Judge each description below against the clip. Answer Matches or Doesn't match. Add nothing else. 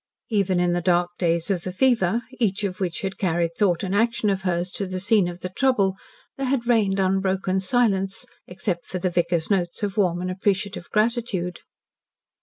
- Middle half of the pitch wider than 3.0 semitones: Doesn't match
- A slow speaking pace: Doesn't match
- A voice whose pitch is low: Doesn't match